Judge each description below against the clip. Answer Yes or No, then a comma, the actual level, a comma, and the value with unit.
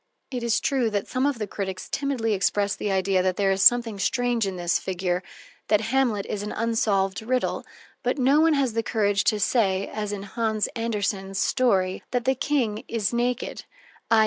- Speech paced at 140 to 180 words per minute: No, average, 190 wpm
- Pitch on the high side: Yes, high, 215 Hz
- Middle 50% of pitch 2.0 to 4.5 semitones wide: Yes, average, 3.8 semitones